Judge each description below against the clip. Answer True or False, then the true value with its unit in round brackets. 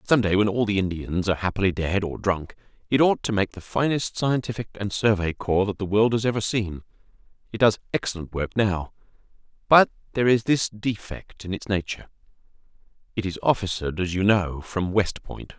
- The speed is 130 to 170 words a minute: False (190 wpm)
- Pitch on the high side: False (100 Hz)